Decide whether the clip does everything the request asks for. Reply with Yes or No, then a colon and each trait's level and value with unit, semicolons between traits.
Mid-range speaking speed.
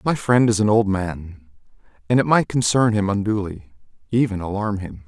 Yes: average, 165 wpm